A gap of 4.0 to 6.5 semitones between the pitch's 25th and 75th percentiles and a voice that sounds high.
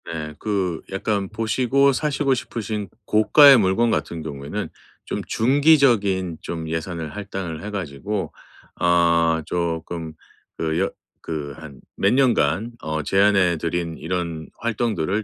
No: average, 5.1 semitones; very low, 95 Hz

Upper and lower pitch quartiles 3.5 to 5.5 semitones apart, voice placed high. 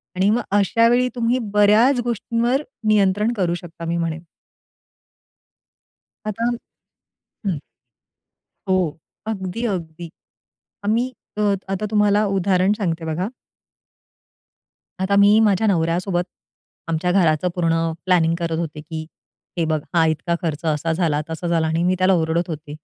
No: average, 4.1 semitones; medium, 180 Hz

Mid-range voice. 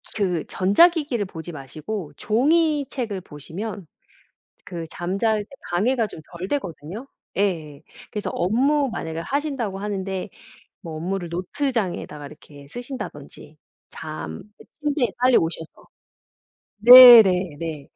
No: high, 195 Hz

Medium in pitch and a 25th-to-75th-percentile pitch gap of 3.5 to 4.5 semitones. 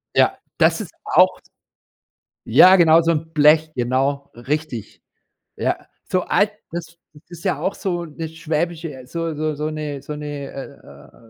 No: medium, 155 Hz; average, 2.7 semitones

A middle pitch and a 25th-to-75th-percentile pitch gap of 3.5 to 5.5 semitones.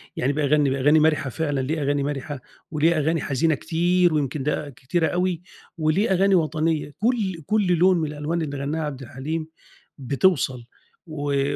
No: medium, 155 Hz; average, 2.9 semitones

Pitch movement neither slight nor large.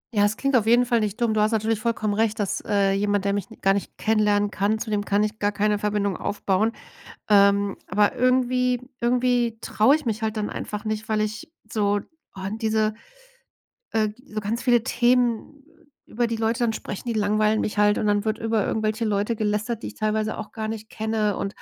No: narrow, 1.7 semitones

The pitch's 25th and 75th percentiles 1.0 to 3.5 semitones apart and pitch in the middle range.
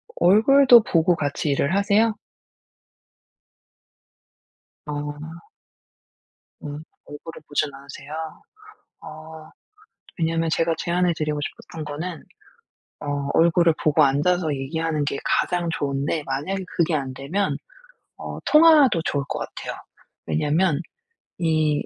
Yes: average, 3.2 semitones; medium, 160 Hz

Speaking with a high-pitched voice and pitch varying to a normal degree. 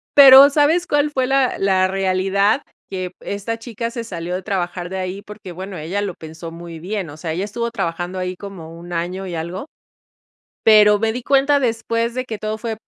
Yes: high, 200 Hz; average, 4.5 semitones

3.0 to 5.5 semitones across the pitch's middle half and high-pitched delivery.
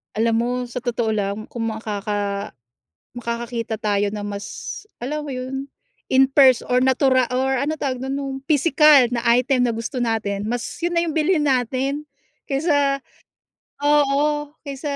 Yes: average, 3.7 semitones; very high, 255 Hz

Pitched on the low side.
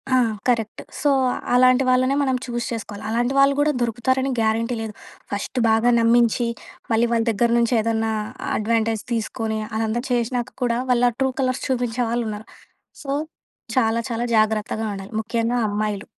No: high, 230 Hz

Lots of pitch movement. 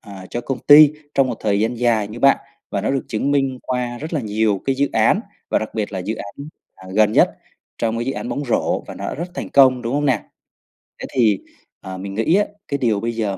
No: average, 4.4 semitones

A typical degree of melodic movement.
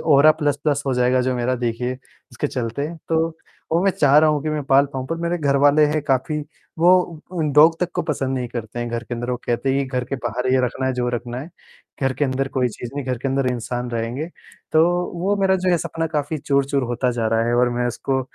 Yes: average, 3.4 semitones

